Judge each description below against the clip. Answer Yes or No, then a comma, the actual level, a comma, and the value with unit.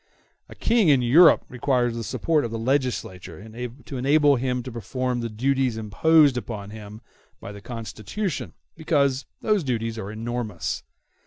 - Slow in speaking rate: No, average, 150 wpm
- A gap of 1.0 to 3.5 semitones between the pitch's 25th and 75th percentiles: No, average, 4.0 semitones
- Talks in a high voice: No, low, 125 Hz